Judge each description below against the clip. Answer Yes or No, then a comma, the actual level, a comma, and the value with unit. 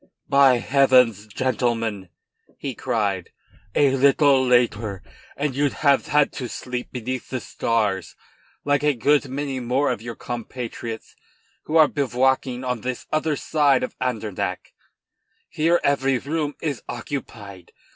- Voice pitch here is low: Yes, low, 130 Hz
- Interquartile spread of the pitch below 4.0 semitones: Yes, average, 3.4 semitones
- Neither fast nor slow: No, slow, 130 wpm